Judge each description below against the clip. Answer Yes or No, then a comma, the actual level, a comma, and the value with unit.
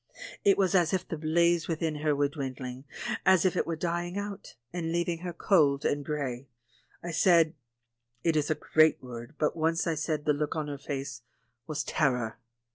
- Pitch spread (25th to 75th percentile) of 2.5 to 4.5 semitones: Yes, average, 3.1 semitones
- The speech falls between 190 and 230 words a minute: Yes, average, 195 wpm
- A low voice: No, medium, 155 Hz